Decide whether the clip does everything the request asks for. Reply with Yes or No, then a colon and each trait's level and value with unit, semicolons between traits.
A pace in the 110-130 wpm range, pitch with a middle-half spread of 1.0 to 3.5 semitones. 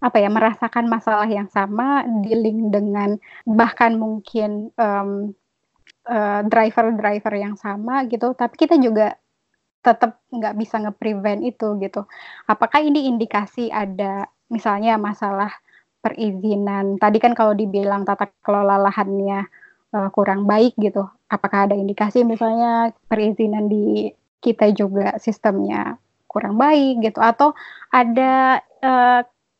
Yes: average, 120 wpm; narrow, 2.4 semitones